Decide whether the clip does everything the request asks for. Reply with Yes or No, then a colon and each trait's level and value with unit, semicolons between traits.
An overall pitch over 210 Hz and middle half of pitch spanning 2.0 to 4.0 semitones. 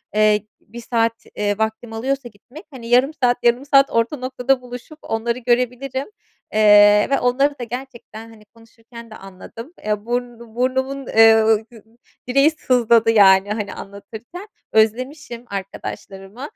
Yes: high, 235 Hz; average, 2.8 semitones